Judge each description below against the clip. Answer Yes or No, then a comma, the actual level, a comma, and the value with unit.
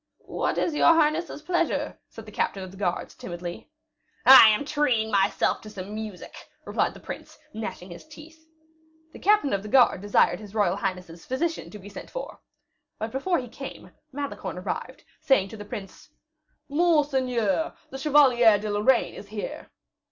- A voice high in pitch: Yes, high, 225 Hz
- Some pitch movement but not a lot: No, wide, 6.5 semitones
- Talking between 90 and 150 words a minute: No, average, 165 wpm